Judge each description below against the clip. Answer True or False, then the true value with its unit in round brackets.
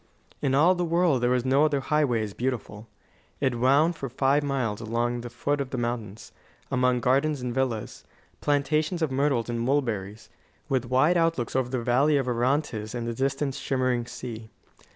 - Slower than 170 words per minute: False (175 wpm)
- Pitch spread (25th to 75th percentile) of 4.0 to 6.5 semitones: False (3.1 semitones)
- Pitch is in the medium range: False (130 Hz)